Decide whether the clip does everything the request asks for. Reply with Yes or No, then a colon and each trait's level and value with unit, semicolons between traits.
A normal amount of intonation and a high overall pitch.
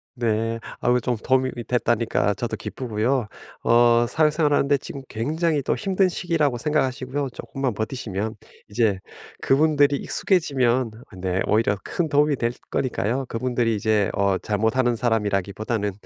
No: average, 4.1 semitones; low, 120 Hz